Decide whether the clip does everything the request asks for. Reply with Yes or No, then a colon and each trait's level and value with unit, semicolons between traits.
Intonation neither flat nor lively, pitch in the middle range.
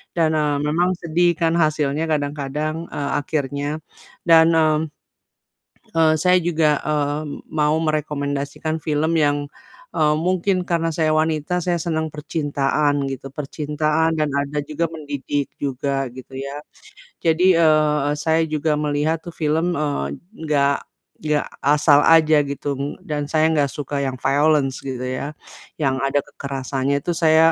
No: narrow, 1.9 semitones; medium, 150 Hz